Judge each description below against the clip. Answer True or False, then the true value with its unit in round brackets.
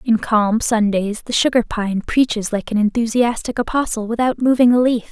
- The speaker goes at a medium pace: True (190 wpm)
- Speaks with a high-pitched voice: True (230 Hz)